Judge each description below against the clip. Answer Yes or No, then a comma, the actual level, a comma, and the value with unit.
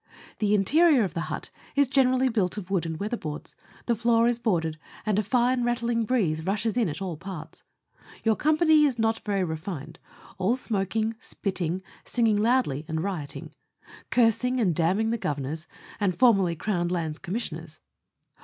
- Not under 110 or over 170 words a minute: Yes, average, 165 wpm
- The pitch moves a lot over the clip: Yes, wide, 5.7 semitones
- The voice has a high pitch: Yes, high, 205 Hz